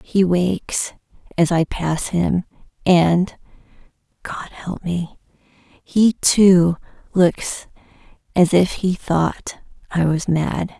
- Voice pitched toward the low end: No, medium, 175 Hz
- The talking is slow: Yes, slow, 110 wpm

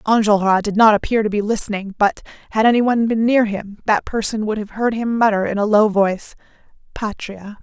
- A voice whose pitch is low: No, high, 215 Hz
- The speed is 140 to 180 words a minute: No, fast, 205 wpm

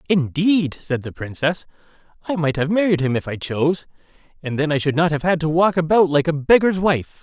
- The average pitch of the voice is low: No, medium, 160 Hz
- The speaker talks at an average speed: No, fast, 215 wpm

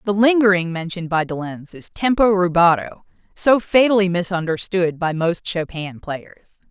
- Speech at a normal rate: Yes, average, 145 wpm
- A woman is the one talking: Yes, female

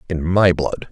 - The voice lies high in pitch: No, very low, 90 Hz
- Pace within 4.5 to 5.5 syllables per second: Yes, 5.2 syllables/s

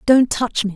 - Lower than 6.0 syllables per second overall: Yes, 4.8 syllables/s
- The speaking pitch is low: No, high, 230 Hz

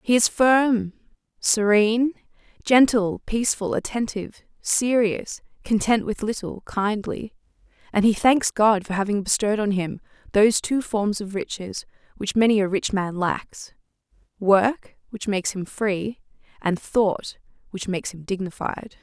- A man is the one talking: No, female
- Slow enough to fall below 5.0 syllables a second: Yes, 4.4 syllables/s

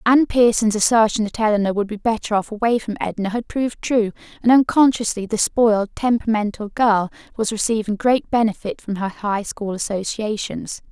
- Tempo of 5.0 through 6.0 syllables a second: Yes, 5.5 syllables/s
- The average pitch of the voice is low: No, high, 220 Hz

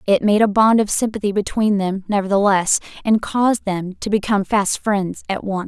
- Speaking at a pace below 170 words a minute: No, average, 190 wpm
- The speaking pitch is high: Yes, high, 205 Hz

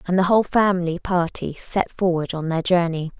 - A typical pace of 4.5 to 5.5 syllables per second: Yes, 5.4 syllables/s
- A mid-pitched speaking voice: Yes, medium, 175 Hz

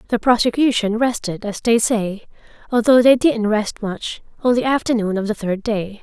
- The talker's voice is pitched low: No, high, 225 Hz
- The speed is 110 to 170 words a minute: No, average, 180 wpm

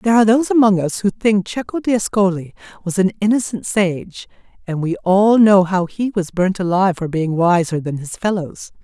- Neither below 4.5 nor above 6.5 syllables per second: Yes, 5.2 syllables/s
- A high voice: Yes, high, 195 Hz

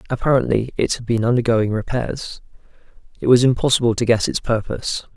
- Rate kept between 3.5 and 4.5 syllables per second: No, 5.9 syllables/s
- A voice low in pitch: Yes, low, 120 Hz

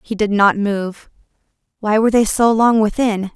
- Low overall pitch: No, high, 215 Hz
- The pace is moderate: Yes, average, 180 wpm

